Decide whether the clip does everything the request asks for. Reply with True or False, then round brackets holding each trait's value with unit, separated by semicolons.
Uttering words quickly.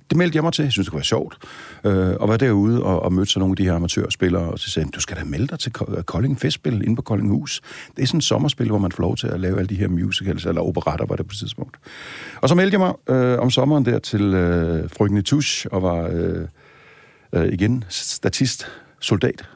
True (250 wpm)